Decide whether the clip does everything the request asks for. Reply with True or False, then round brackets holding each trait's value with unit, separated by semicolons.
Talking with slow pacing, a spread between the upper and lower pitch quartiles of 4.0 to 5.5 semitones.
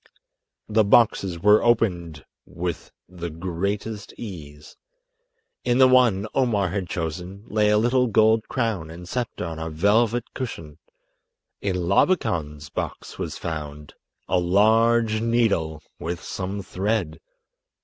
True (120 wpm; 5.1 semitones)